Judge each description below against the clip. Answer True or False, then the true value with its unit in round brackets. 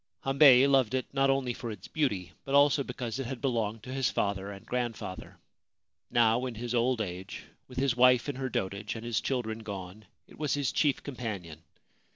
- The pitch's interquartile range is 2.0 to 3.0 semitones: False (3.8 semitones)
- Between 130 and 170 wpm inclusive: False (195 wpm)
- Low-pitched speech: True (120 Hz)